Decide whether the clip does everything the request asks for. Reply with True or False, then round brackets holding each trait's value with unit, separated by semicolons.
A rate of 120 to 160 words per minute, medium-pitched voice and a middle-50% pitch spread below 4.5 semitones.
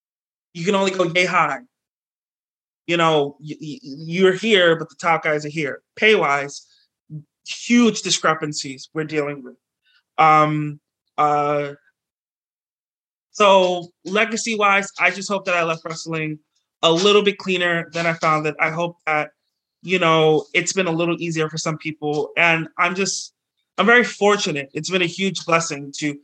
True (155 wpm; 165 Hz; 3.4 semitones)